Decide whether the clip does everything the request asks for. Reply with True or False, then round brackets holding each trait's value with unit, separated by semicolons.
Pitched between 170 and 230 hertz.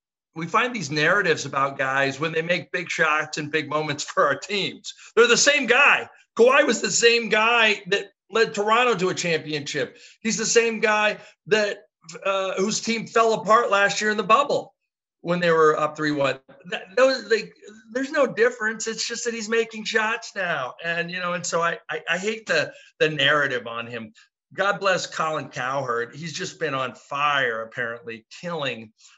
True (190 Hz)